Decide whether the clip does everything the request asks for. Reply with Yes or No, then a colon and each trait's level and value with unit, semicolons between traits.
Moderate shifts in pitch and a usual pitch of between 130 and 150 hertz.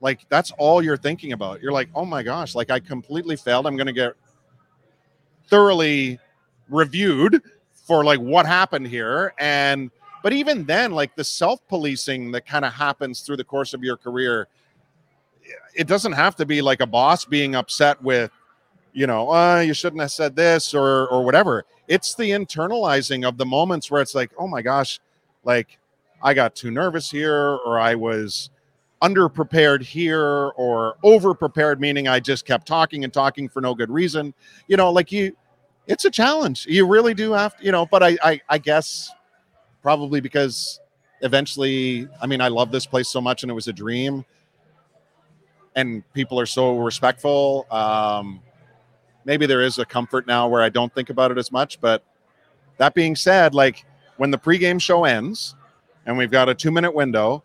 Yes: average, 4.3 semitones; medium, 140 Hz